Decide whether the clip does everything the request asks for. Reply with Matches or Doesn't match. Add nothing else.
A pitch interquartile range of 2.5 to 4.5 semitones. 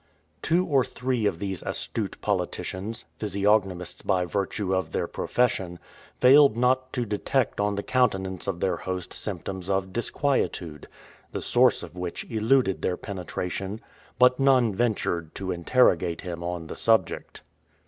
Doesn't match